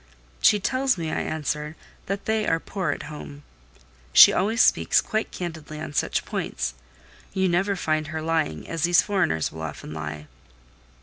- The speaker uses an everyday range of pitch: Yes, average, 4.6 semitones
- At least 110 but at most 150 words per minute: No, average, 165 wpm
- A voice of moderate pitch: Yes, medium, 160 Hz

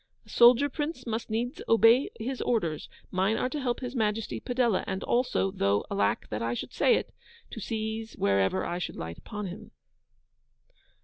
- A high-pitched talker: Yes, high, 220 Hz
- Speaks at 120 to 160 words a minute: No, average, 175 wpm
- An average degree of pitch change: No, wide, 6.2 semitones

